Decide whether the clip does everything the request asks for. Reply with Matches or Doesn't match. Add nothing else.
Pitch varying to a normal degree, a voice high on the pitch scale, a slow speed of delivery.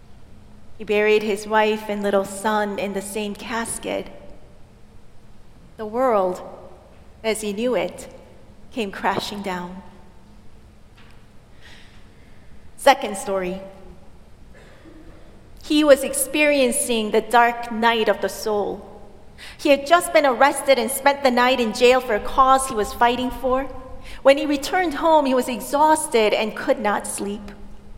Matches